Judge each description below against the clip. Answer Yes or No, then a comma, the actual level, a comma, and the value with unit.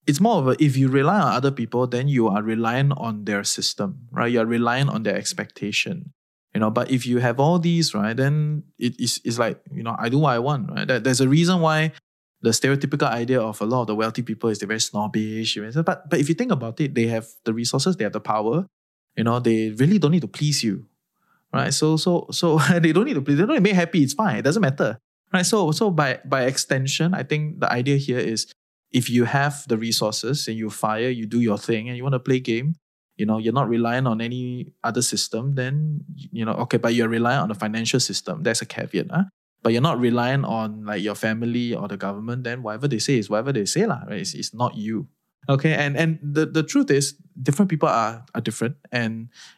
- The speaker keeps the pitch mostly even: No, average, 5.0 semitones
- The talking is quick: Yes, fast, 245 wpm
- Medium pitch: No, low, 125 Hz